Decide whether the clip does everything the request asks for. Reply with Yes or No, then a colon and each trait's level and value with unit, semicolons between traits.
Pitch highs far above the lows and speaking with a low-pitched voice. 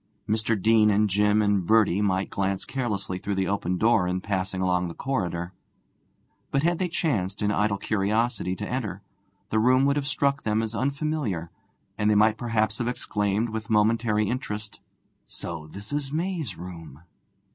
No: average, 3.7 semitones; low, 105 Hz